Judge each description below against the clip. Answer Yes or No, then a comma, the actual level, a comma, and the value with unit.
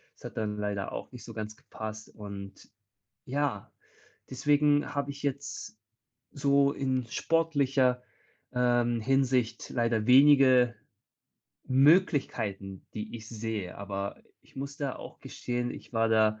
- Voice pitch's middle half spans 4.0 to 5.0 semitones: Yes, average, 4.3 semitones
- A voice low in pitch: Yes, low, 125 Hz